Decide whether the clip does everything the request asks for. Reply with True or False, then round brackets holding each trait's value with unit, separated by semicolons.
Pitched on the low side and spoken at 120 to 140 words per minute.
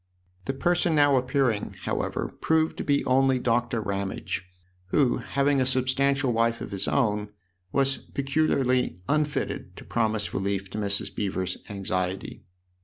True (125 Hz; 135 wpm)